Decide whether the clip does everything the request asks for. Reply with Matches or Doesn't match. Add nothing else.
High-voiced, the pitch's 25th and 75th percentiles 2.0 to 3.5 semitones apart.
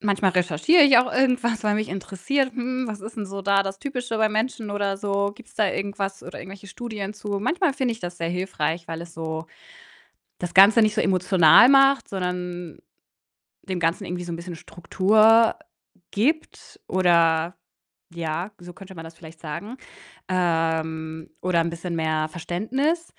Doesn't match